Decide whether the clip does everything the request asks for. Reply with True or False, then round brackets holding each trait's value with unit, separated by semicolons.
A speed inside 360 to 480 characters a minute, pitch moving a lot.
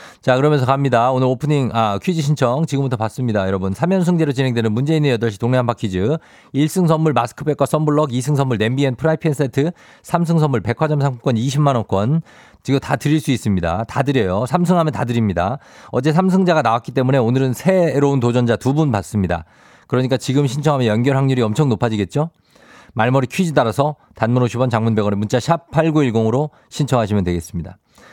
False (390 characters per minute; 4.6 semitones)